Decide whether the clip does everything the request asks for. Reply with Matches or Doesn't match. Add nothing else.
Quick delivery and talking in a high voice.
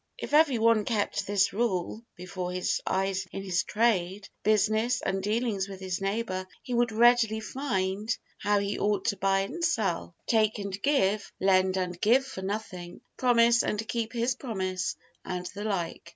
Doesn't match